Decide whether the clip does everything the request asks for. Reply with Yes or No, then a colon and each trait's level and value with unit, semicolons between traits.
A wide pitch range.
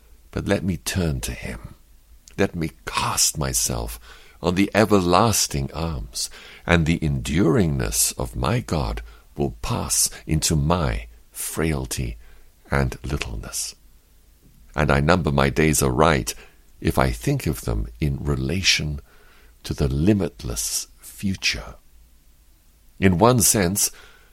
No: average, 3.8 semitones